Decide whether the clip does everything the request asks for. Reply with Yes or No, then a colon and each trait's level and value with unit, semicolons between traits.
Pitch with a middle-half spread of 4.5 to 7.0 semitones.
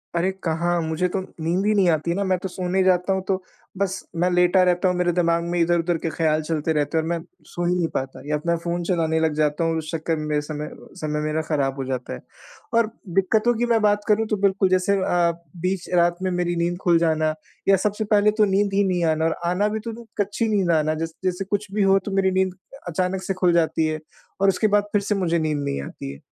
No: average, 3.1 semitones